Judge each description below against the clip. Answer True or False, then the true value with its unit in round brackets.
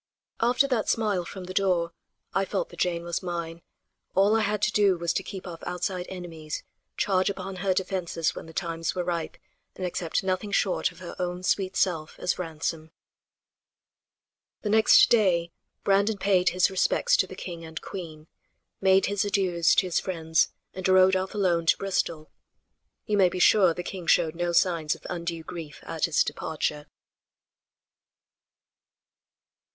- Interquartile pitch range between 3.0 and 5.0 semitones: False (2.5 semitones)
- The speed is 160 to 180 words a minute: True (165 wpm)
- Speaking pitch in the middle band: True (180 Hz)